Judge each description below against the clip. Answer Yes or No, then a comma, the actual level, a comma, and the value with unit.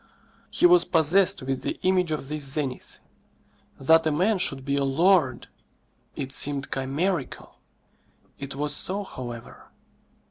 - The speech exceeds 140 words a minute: No, slow, 135 wpm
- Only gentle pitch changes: No, average, 5.3 semitones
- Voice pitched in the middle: Yes, medium, 150 Hz